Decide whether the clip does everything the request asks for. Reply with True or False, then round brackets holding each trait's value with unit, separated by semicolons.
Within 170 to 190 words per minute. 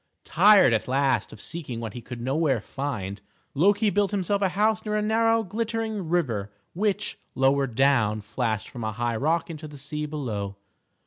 True (175 wpm)